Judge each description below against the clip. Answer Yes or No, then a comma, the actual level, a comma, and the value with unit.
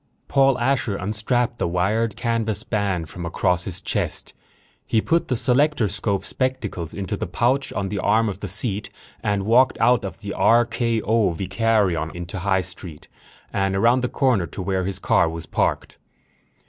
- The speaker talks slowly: No, average, 160 wpm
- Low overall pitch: Yes, low, 105 Hz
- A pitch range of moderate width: Yes, average, 4.0 semitones